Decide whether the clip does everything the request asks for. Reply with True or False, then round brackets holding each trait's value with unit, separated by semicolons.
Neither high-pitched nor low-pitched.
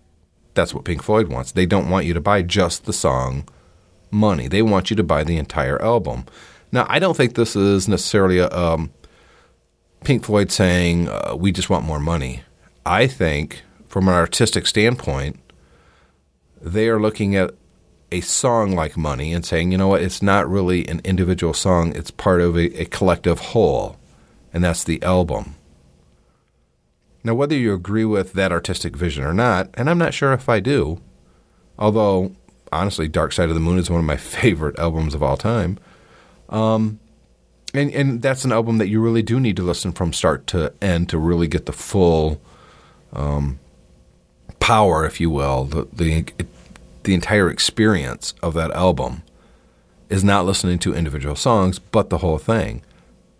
False (90 Hz)